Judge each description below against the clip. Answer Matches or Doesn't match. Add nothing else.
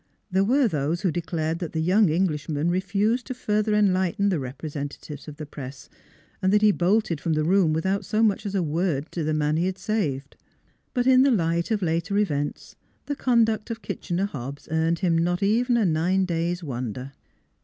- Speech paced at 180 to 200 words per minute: Matches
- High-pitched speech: Doesn't match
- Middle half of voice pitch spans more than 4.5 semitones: Matches